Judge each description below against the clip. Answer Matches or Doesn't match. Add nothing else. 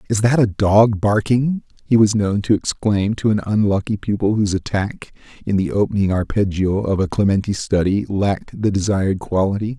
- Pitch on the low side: Matches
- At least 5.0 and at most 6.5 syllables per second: Matches